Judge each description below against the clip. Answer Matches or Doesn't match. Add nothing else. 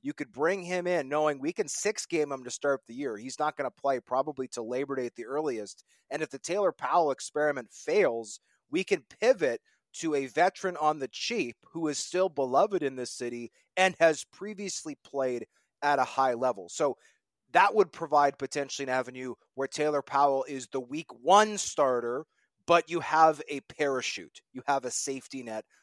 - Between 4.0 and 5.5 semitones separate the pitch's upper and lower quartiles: Matches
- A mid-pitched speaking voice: Matches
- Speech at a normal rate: Matches